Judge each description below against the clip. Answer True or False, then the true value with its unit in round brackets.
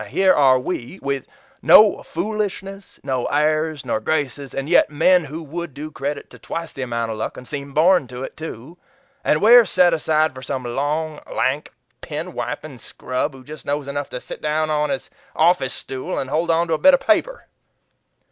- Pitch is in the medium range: True (150 Hz)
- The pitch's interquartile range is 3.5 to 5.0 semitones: True (3.8 semitones)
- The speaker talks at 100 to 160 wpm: False (195 wpm)